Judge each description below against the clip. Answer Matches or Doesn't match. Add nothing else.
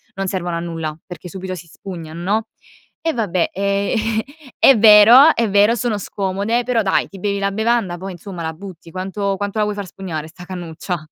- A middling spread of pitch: Matches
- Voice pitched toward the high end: Matches